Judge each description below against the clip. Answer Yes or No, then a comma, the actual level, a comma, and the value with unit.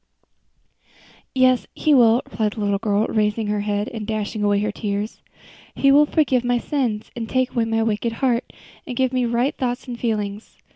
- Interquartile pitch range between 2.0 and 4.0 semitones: Yes, average, 3.1 semitones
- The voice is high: Yes, high, 225 Hz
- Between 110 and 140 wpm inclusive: No, average, 185 wpm